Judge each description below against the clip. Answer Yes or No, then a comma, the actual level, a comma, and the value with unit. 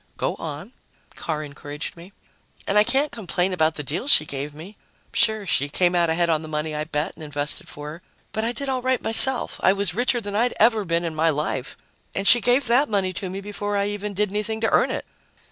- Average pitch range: No, wide, 5.8 semitones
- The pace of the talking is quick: Yes, fast, 230 wpm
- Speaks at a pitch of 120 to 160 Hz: No, high, 190 Hz